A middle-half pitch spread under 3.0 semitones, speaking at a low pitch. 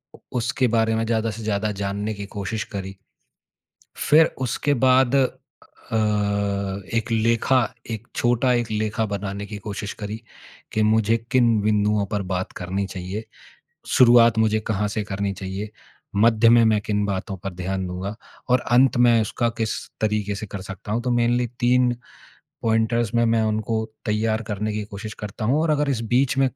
Yes: narrow, 2.5 semitones; low, 110 Hz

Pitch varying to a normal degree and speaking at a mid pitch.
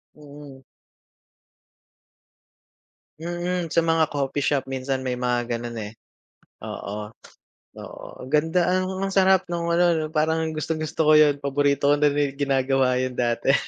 Yes: average, 3.6 semitones; medium, 145 Hz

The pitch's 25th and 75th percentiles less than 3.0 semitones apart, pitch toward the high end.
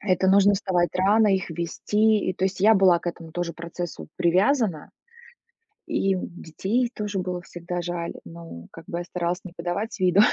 No: narrow, 2.4 semitones; medium, 180 Hz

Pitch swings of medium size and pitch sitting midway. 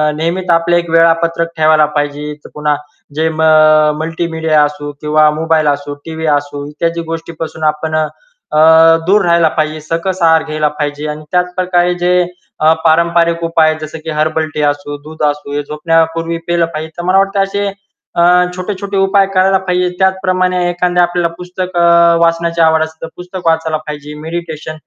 No: narrow, 2.3 semitones; medium, 165 Hz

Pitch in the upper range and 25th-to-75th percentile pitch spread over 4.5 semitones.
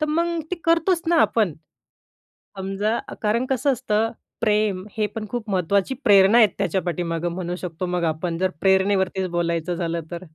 No: high, 195 Hz; average, 4.2 semitones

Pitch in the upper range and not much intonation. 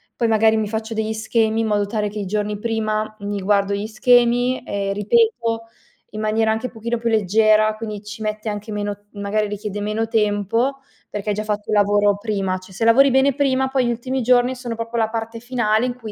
Yes: high, 220 Hz; narrow, 1.9 semitones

